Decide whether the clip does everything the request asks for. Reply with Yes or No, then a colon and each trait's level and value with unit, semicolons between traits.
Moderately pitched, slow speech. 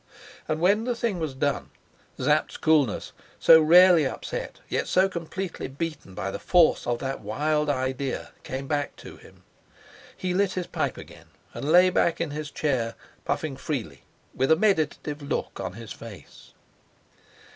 No: medium, 155 Hz; average, 155 wpm